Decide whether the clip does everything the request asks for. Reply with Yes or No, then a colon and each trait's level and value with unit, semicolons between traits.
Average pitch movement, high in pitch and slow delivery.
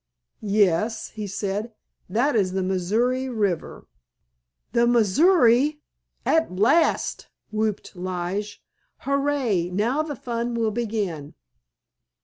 Yes: average, 4.3 semitones; high, 220 Hz; slow, 95 wpm